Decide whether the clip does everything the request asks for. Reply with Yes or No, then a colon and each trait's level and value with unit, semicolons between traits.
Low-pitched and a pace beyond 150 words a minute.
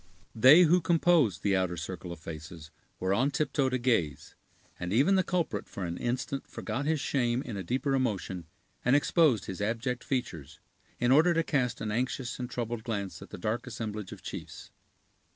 Yes: low, 120 Hz; average, 185 wpm